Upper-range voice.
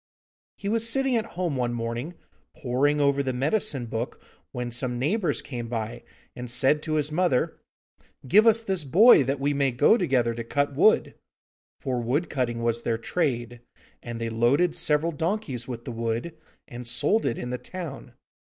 No: low, 135 Hz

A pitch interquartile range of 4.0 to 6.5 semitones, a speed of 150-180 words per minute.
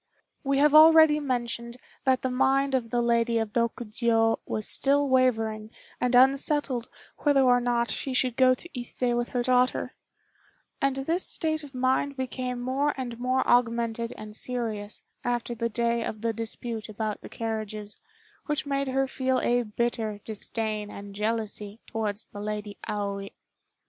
No: average, 2.8 semitones; average, 155 wpm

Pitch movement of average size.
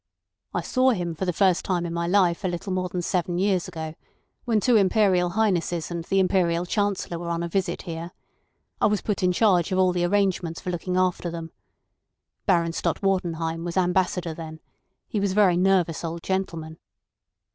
No: narrow, 2.2 semitones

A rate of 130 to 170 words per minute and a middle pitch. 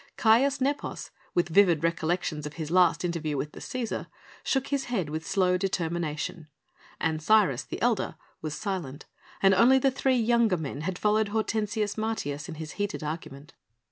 Yes: average, 160 wpm; medium, 180 Hz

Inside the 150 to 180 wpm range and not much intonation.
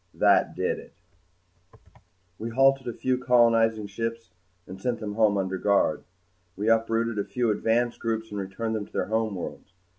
Yes: average, 160 wpm; narrow, 2.2 semitones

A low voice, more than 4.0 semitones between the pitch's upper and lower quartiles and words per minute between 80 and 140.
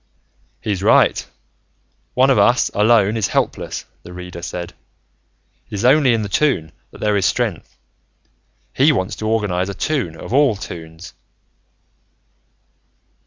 Yes: low, 105 Hz; average, 5.1 semitones; slow, 135 wpm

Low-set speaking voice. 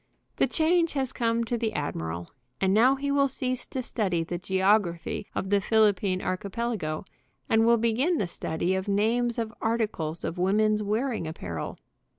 No: high, 215 Hz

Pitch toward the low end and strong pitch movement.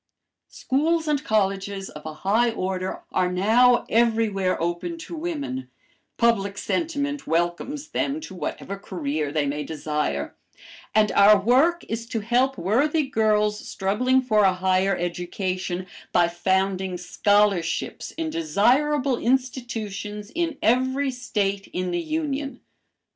No: high, 210 Hz; wide, 6.0 semitones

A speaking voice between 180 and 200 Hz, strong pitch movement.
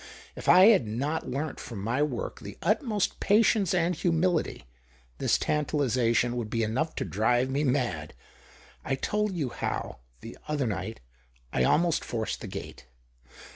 No: medium, 140 Hz; wide, 6.8 semitones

